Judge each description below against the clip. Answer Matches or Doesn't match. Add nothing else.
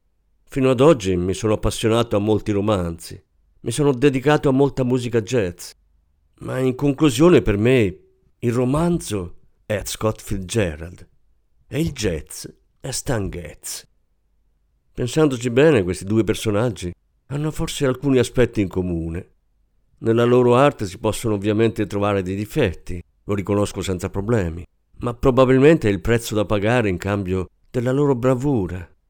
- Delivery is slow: Doesn't match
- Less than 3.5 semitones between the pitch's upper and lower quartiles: Doesn't match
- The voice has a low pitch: Matches